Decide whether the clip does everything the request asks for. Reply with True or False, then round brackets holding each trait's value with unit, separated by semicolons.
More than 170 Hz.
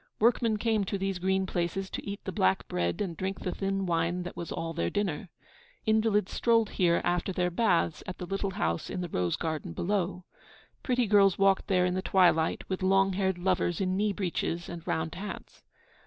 True (185 Hz)